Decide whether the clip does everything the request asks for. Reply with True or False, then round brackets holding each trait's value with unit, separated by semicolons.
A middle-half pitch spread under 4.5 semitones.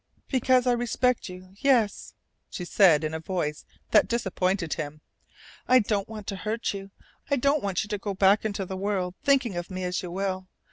True (3.8 semitones)